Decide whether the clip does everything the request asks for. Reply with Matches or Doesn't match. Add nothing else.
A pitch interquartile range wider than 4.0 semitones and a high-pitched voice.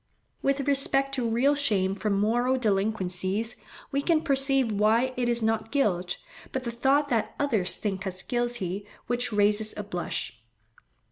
Matches